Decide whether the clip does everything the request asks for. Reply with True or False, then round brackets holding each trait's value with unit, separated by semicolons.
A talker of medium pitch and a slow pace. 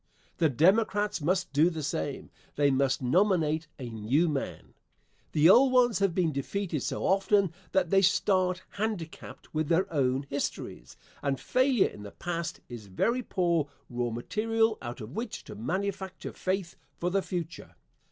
False (175 Hz; 155 wpm)